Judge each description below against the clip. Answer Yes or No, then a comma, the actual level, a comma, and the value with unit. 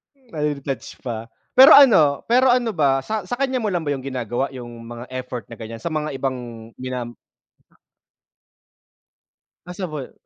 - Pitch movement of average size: No, wide, 7.0 semitones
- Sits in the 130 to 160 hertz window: Yes, medium, 140 Hz